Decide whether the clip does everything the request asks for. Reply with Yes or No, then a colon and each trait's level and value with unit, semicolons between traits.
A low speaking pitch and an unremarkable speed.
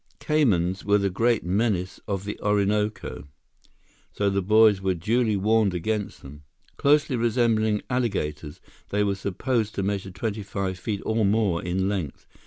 Yes: low, 100 Hz; average, 150 wpm